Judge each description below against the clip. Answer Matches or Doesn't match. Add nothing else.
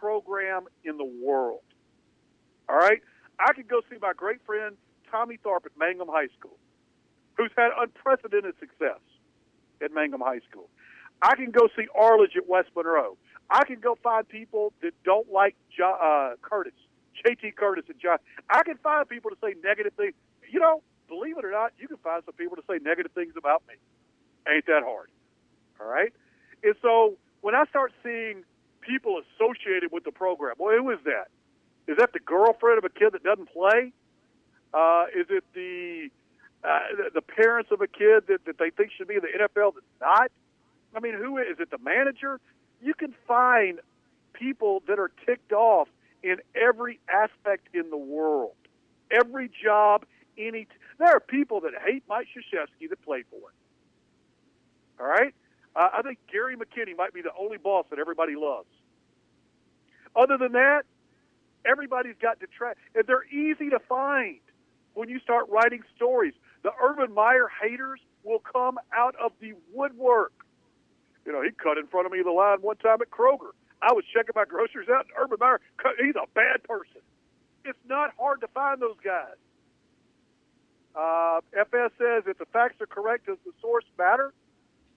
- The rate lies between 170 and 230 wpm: Matches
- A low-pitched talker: Doesn't match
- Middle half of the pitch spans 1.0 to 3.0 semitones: Doesn't match